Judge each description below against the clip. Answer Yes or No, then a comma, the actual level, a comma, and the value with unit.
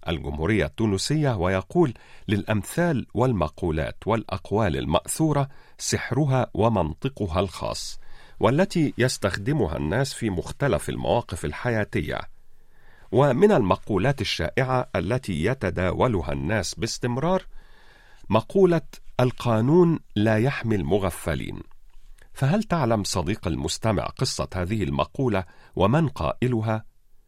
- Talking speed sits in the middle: Yes, average, 85 wpm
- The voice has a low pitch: Yes, low, 110 Hz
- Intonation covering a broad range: Yes, wide, 6.1 semitones